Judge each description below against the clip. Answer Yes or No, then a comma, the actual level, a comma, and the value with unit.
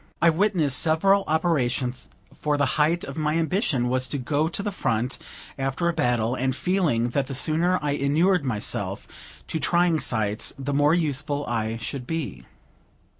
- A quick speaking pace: No, average, 165 wpm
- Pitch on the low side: No, medium, 145 Hz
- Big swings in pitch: No, average, 4.5 semitones